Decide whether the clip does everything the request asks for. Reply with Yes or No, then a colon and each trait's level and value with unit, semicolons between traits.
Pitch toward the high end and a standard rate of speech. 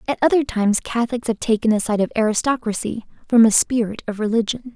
Yes: high, 225 Hz; average, 190 wpm